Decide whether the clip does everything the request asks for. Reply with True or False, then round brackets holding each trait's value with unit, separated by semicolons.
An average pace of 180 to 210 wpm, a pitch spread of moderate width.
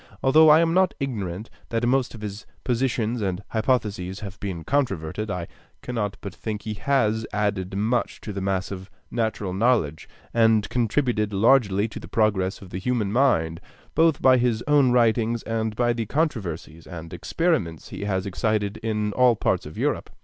False (170 wpm; 4.0 semitones)